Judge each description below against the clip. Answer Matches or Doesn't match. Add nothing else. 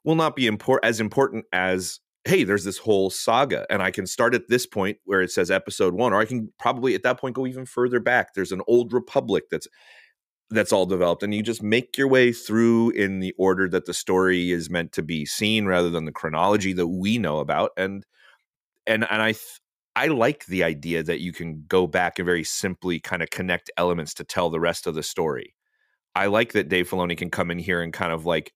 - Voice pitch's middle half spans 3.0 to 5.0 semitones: Matches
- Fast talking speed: Matches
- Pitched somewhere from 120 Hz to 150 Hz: Doesn't match